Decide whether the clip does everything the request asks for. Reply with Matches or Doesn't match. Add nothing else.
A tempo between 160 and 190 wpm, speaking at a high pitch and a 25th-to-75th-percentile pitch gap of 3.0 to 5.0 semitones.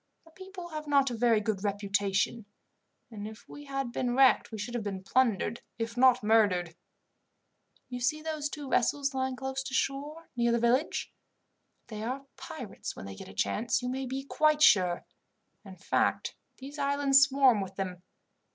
Matches